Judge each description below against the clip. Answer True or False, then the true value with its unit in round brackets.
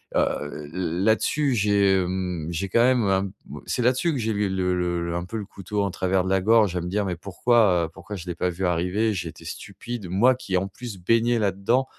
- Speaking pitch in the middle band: False (95 Hz)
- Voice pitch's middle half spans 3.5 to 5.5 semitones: True (3.8 semitones)